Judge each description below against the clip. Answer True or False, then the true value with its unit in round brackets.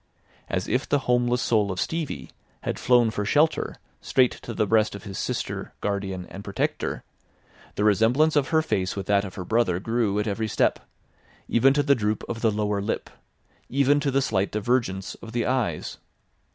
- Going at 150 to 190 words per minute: True (185 wpm)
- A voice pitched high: False (110 Hz)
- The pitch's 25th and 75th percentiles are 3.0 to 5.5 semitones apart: True (4.0 semitones)